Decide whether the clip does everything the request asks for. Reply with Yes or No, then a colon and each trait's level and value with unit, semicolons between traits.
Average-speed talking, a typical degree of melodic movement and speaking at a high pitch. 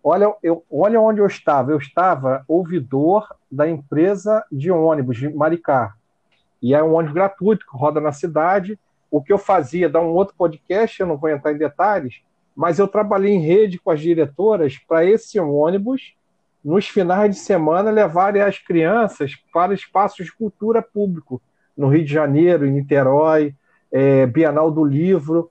No: average, 165 wpm; average, 4.9 semitones; medium, 165 Hz